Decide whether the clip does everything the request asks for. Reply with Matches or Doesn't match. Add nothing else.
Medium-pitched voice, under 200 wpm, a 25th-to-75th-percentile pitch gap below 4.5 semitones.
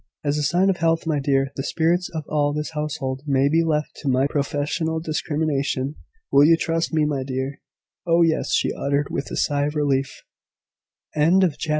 Doesn't match